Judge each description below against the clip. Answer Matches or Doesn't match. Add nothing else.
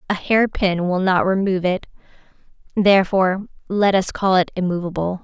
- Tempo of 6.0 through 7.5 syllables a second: Doesn't match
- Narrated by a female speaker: Matches